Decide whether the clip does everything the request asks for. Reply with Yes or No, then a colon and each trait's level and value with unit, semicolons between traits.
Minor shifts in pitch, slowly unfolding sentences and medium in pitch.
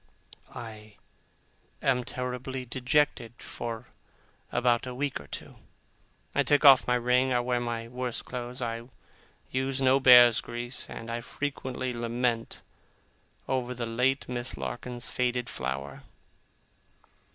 No: narrow, 1.5 semitones; slow, 125 wpm; low, 125 Hz